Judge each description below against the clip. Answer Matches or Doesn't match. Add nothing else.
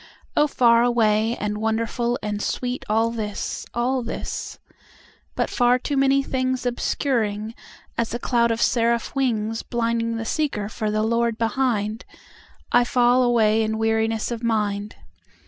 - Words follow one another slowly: Matches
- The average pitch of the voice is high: Matches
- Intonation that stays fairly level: Matches